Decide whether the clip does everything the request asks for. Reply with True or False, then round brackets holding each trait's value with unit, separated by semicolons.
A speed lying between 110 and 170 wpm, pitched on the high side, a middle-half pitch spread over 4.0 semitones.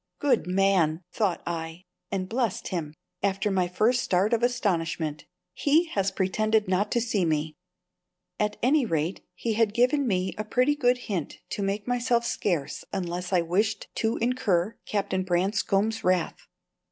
True (155 wpm; 200 Hz; 4.5 semitones)